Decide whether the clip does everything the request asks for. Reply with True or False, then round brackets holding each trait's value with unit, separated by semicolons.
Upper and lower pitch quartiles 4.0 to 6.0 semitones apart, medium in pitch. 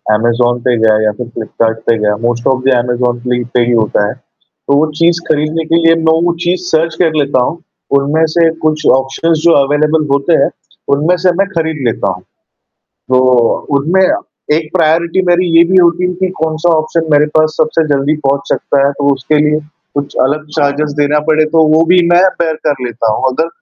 True (4.4 semitones; 150 Hz)